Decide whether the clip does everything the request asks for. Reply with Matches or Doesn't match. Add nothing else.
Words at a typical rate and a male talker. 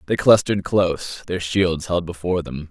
Matches